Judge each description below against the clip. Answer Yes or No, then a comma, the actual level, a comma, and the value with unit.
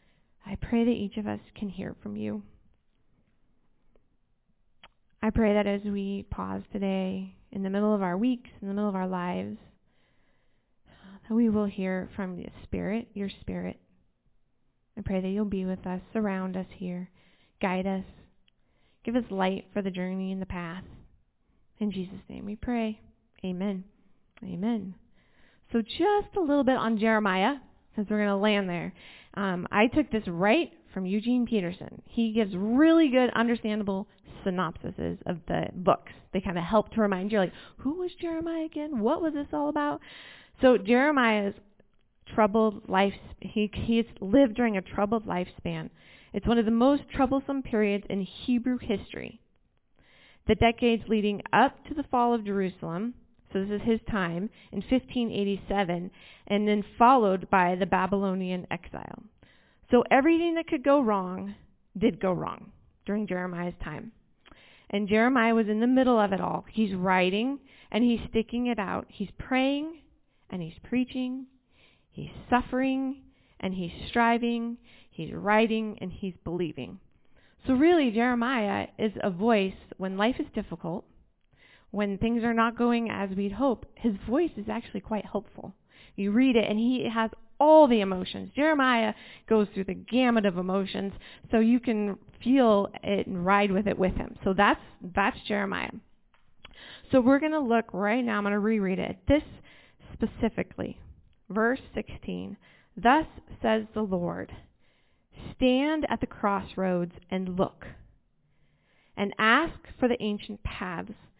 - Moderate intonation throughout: Yes, average, 3.8 semitones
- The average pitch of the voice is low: No, high, 215 Hz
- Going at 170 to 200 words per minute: No, average, 155 wpm